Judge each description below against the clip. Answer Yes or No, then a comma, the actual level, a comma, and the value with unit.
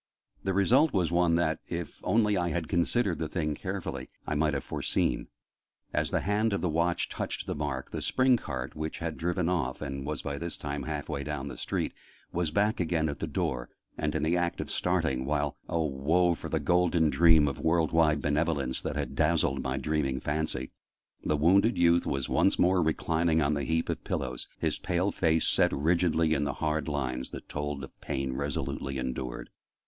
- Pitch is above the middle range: No, very low, 80 Hz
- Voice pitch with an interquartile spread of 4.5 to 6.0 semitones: No, average, 3.3 semitones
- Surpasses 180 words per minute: Yes, average, 200 wpm